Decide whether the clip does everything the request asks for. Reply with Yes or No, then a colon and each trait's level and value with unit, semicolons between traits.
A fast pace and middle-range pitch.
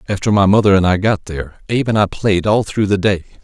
No: fast, 260 wpm; low, 100 Hz